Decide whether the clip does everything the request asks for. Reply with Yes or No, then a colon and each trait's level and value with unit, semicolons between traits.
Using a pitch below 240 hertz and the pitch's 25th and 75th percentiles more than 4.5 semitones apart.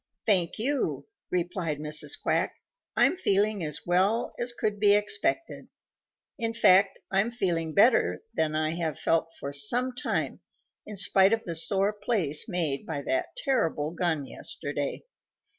Yes: medium, 185 Hz; wide, 5.4 semitones